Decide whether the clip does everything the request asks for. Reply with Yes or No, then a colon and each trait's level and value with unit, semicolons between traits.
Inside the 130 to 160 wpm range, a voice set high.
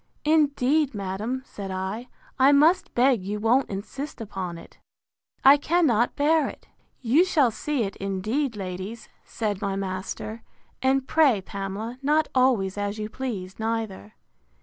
Yes: slow, 135 wpm; high, 225 Hz